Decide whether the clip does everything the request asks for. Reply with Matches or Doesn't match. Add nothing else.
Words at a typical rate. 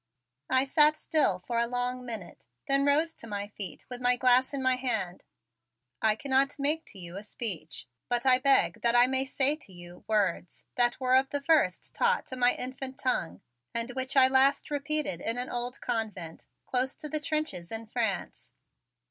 Matches